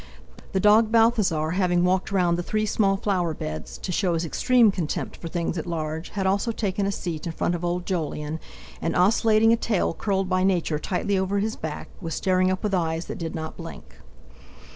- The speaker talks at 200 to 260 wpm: Yes, fast, 205 wpm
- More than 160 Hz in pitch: Yes, medium, 185 Hz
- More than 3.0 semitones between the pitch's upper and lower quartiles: Yes, average, 3.4 semitones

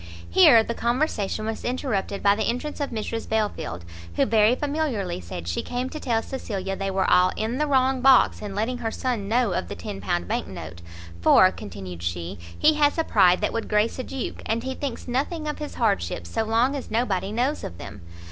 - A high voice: Yes, high, 225 Hz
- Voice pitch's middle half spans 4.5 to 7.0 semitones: Yes, average, 5.1 semitones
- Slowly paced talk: No, fast, 205 wpm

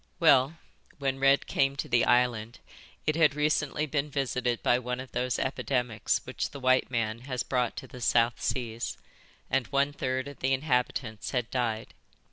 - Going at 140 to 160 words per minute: No, average, 170 wpm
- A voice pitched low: Yes, low, 130 Hz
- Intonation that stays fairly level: Yes, narrow, 2.2 semitones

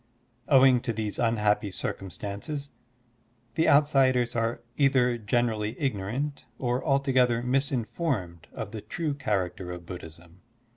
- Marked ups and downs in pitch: No, average, 4.9 semitones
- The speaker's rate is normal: No, slow, 115 wpm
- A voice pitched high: No, low, 120 Hz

